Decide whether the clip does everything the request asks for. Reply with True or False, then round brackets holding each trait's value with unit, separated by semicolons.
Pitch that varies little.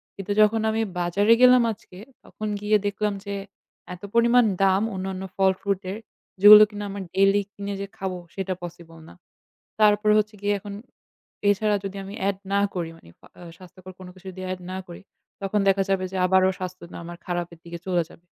True (2.0 semitones)